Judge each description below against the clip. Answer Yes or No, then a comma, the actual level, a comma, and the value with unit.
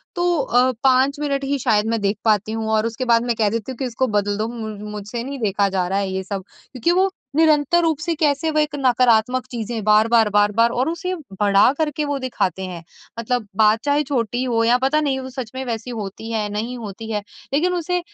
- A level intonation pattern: No, average, 4.5 semitones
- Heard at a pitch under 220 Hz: No, high, 235 Hz